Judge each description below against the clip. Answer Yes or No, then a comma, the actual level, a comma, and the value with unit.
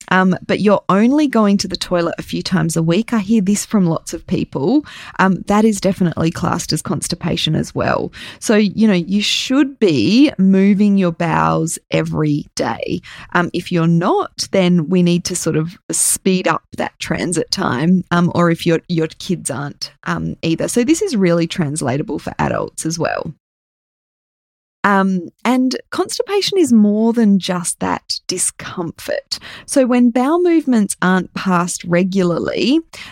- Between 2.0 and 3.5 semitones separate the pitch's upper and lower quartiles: No, average, 4.6 semitones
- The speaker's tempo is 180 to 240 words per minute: No, average, 160 wpm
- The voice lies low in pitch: No, medium, 185 Hz